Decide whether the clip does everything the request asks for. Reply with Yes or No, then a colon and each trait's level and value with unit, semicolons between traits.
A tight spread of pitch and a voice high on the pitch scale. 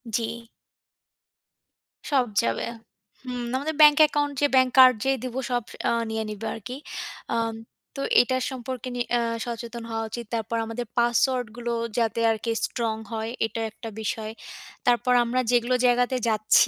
Yes: narrow, 2.1 semitones; high, 240 Hz